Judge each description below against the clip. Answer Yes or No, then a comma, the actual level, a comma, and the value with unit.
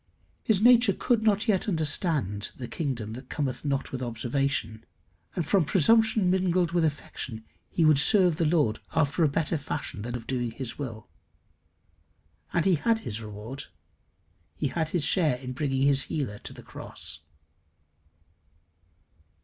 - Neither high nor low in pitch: Yes, medium, 145 Hz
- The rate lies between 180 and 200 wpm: No, average, 155 wpm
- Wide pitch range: Yes, wide, 6.0 semitones